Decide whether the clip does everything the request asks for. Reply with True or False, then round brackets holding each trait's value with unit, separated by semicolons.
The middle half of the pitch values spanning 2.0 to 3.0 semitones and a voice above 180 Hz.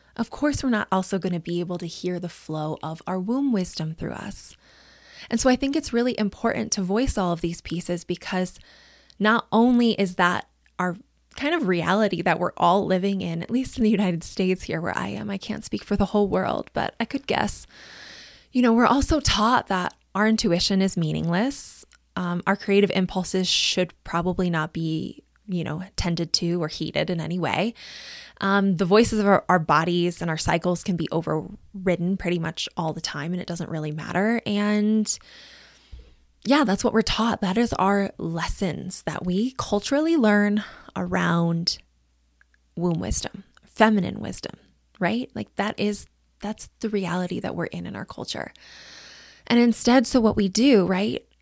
False (4.0 semitones; 190 Hz)